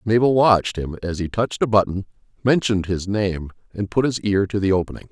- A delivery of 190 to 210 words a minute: Yes, average, 200 wpm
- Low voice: Yes, low, 100 Hz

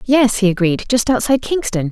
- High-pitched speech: Yes, high, 225 Hz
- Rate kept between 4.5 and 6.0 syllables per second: Yes, 5.7 syllables/s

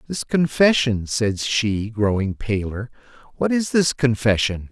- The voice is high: No, low, 120 Hz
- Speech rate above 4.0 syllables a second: No, 3.9 syllables/s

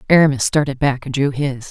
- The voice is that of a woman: Yes, female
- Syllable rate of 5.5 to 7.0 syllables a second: Yes, 5.9 syllables/s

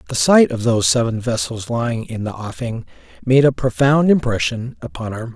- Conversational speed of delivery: Yes, average, 190 wpm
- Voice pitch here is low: Yes, low, 120 Hz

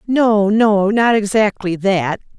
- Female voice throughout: Yes, female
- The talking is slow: Yes, slow, 125 wpm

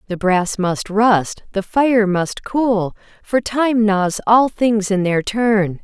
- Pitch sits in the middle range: No, high, 210 Hz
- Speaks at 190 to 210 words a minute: No, average, 165 wpm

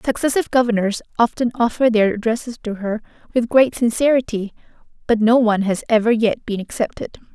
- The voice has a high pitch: Yes, high, 230 Hz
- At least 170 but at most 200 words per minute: No, average, 155 wpm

